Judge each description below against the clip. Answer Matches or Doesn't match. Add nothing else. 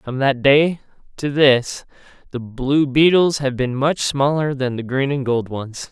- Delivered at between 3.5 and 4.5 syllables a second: Matches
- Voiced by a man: Matches